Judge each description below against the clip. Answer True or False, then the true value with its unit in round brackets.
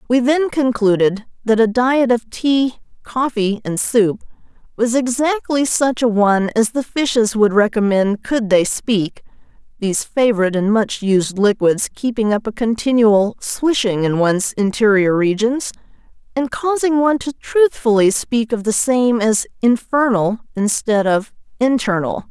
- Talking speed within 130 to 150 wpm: True (145 wpm)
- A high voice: True (225 Hz)